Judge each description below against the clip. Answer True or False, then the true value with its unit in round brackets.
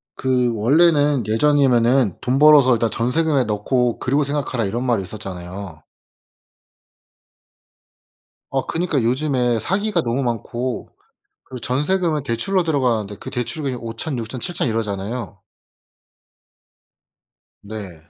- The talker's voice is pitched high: False (125 Hz)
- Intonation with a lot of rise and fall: False (4.3 semitones)